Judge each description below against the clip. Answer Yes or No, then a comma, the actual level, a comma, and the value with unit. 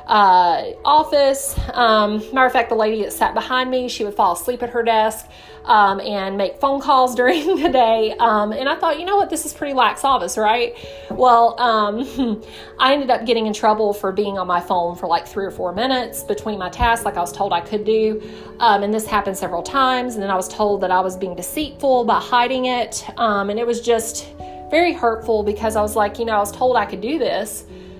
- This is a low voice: No, high, 225 Hz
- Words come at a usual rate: No, fast, 230 wpm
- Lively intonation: No, average, 3.8 semitones